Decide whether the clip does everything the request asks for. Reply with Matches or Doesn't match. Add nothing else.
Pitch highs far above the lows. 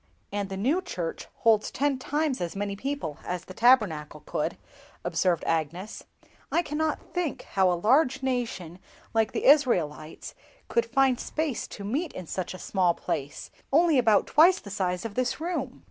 Matches